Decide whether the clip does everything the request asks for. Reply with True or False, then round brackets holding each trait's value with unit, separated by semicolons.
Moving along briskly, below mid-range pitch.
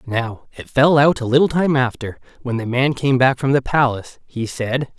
True (215 wpm; 130 Hz)